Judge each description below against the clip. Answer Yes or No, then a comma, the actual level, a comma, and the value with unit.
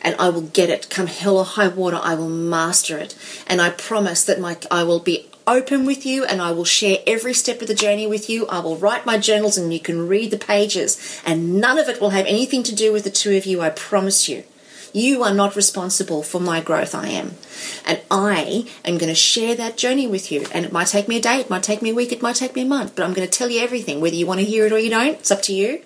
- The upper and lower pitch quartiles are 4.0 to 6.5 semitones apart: Yes, average, 4.3 semitones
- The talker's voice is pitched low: No, high, 200 Hz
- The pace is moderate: No, fast, 285 wpm